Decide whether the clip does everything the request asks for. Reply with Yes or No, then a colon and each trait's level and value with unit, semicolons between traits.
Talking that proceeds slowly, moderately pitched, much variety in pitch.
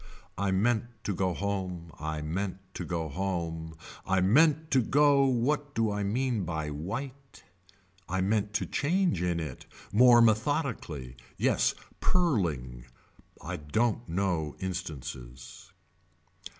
No: slow, 125 wpm; very low, 95 Hz; wide, 6.8 semitones